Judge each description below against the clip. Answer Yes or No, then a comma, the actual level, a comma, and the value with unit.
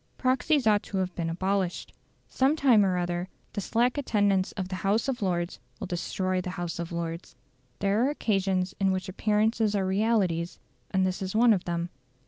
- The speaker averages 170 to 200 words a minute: Yes, average, 185 wpm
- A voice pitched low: No, high, 190 Hz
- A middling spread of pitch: Yes, average, 3.1 semitones